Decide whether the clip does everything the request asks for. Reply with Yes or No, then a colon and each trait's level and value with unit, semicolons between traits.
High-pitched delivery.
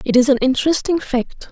Yes: very high, 270 Hz